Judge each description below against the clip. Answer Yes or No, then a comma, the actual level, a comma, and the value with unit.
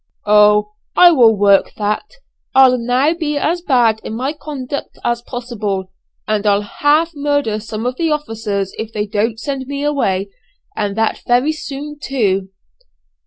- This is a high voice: Yes, high, 240 Hz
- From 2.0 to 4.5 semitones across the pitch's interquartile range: No, wide, 5.5 semitones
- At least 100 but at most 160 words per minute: Yes, average, 155 wpm